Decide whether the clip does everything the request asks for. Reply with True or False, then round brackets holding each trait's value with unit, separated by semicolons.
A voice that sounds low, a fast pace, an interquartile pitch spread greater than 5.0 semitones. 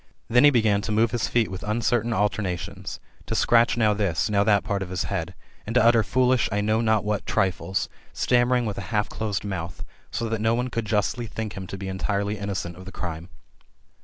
False (105 Hz; 215 wpm; 2.9 semitones)